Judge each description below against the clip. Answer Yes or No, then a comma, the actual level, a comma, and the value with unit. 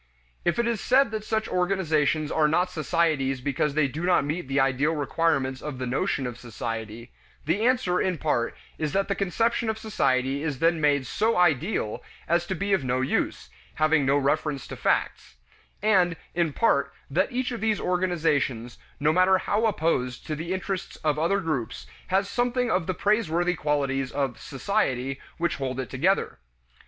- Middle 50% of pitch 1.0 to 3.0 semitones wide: No, wide, 5.6 semitones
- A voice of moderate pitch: Yes, medium, 160 Hz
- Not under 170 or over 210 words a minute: Yes, average, 175 wpm